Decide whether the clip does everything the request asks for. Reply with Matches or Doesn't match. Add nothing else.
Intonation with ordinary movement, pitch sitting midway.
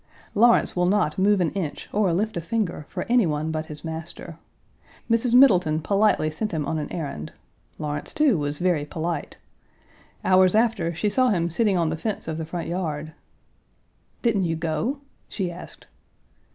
Matches